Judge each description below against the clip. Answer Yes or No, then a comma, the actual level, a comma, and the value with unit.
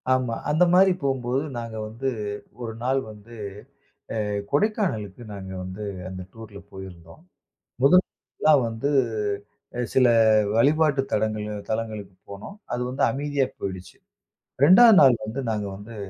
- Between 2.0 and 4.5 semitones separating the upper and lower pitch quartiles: No, average, 5.0 semitones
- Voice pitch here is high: No, low, 115 Hz